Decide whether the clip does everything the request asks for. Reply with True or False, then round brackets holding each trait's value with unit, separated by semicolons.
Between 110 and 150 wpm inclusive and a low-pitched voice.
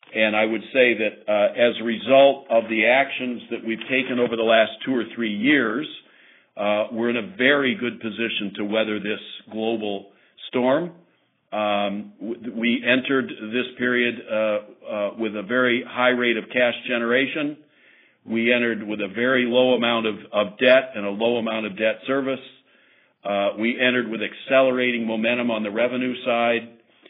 False (170 wpm; 115 Hz)